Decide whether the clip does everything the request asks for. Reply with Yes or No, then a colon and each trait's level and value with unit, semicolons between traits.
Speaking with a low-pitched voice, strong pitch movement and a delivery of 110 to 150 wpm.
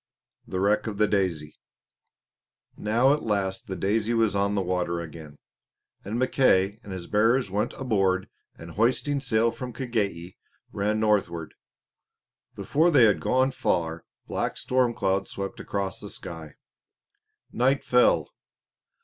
No: low, 105 Hz; average, 4.1 semitones; slow, 135 wpm